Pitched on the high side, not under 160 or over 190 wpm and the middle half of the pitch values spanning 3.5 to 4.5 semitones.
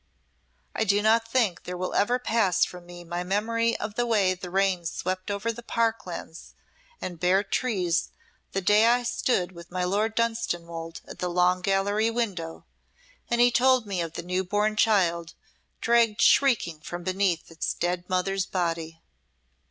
Yes: high, 195 Hz; average, 165 wpm; average, 4.2 semitones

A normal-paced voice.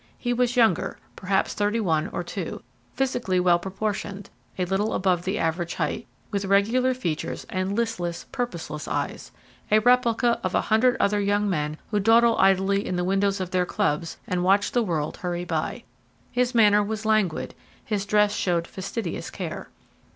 Yes: average, 165 wpm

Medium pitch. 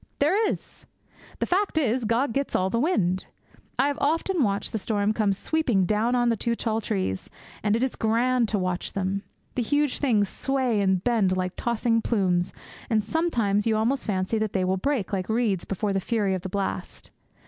No: high, 220 Hz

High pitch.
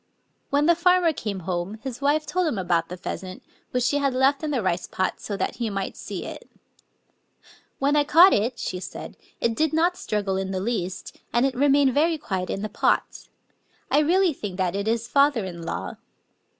Yes: high, 240 Hz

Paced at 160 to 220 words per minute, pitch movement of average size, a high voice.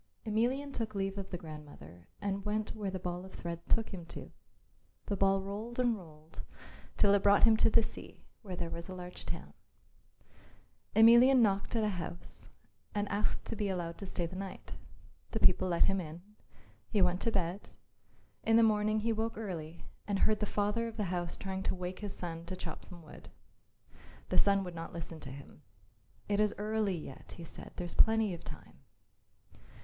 Yes: average, 195 wpm; average, 3.5 semitones; high, 195 Hz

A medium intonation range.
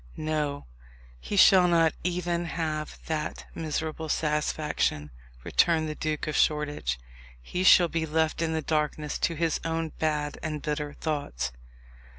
No: narrow, 1.5 semitones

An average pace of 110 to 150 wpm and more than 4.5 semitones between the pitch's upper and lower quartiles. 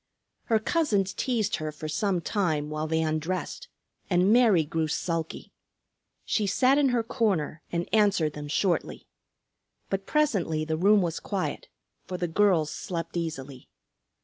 Yes: average, 145 wpm; average, 5.1 semitones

